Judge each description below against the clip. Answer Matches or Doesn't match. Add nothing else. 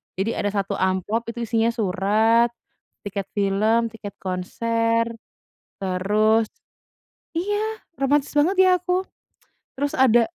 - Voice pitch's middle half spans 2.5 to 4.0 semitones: Doesn't match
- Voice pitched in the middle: Doesn't match